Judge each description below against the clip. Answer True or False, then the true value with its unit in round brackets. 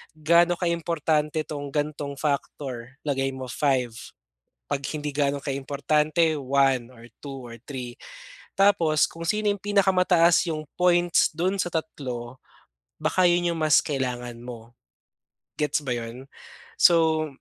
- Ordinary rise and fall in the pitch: True (4.0 semitones)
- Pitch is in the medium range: True (150 Hz)